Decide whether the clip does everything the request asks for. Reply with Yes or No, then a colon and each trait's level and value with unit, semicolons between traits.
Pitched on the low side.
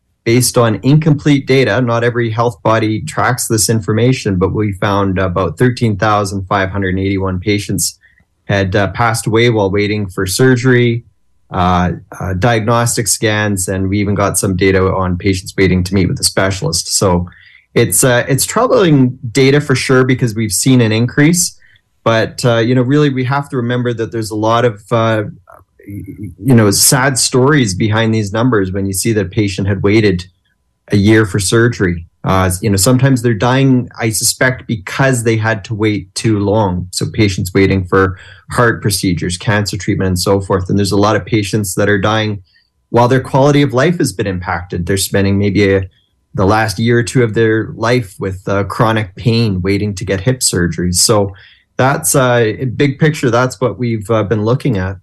Yes: low, 110 Hz